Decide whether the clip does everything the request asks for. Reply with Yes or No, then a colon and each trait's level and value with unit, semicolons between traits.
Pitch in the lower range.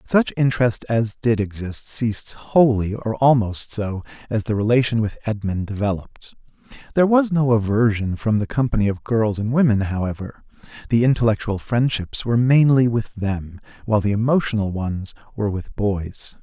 Yes: low, 110 Hz